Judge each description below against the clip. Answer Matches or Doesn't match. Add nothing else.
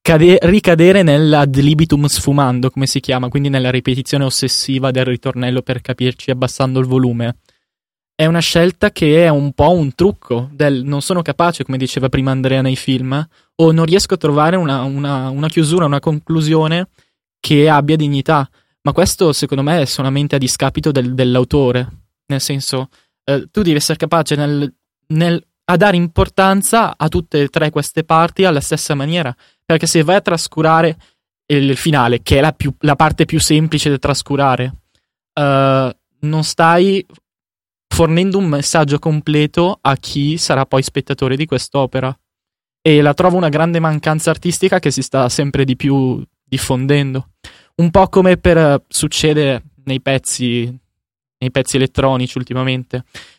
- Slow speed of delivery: Doesn't match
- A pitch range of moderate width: Matches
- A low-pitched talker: Doesn't match